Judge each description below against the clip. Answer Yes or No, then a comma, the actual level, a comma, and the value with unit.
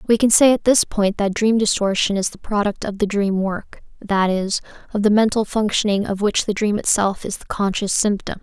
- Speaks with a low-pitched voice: No, high, 205 Hz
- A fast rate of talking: Yes, fast, 220 wpm